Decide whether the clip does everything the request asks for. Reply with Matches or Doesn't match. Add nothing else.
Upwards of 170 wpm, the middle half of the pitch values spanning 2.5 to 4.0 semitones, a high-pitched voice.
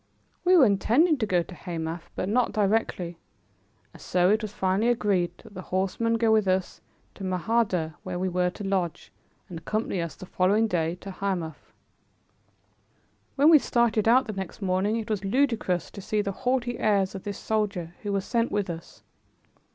Matches